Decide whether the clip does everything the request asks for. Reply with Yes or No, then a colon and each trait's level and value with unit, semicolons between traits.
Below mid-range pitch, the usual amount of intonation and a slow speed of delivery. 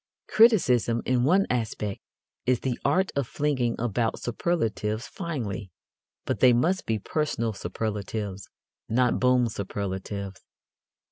Yes: low, 120 Hz; average, 3.9 semitones; slow, 115 wpm